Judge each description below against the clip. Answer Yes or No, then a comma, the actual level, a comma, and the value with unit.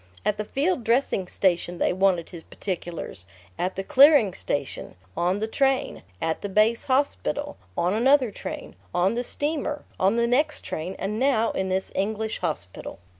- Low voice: No, high, 210 Hz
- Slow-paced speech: No, average, 165 wpm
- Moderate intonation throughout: No, wide, 6.1 semitones